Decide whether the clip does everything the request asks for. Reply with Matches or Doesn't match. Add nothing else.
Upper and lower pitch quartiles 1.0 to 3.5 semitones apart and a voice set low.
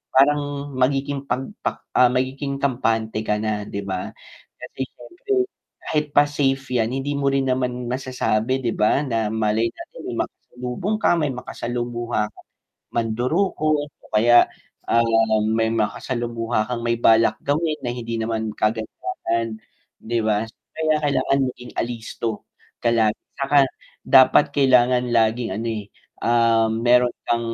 Matches